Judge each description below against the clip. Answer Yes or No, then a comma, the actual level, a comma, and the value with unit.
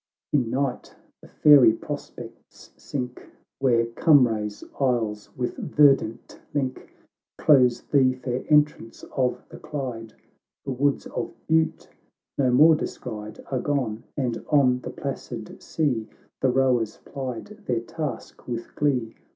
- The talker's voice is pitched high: No, low, 130 Hz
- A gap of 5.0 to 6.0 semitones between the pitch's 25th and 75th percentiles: No, average, 3.4 semitones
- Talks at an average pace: No, slow, 125 wpm